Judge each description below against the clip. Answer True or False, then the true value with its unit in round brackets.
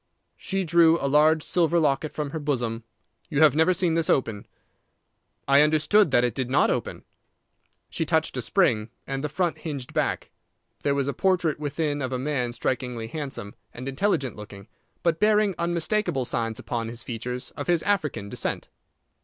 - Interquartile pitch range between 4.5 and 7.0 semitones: True (4.9 semitones)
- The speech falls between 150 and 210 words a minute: True (170 wpm)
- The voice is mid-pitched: True (145 Hz)